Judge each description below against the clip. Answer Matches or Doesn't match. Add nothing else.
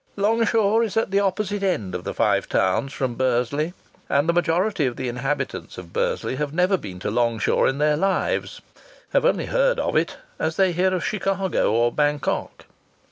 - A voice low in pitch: Doesn't match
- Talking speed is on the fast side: Doesn't match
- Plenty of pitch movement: Matches